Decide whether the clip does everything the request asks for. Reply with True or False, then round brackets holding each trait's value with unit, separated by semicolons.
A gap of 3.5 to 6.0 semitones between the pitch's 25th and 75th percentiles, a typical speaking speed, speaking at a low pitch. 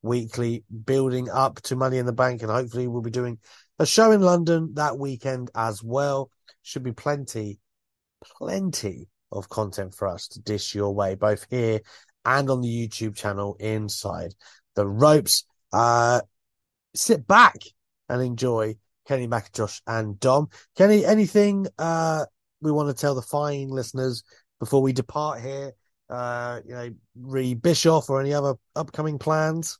True (4.4 semitones; 155 wpm; 125 Hz)